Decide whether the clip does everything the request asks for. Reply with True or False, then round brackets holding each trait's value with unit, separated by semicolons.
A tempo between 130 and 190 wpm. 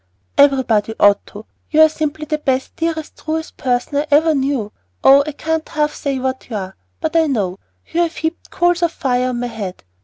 False (205 wpm)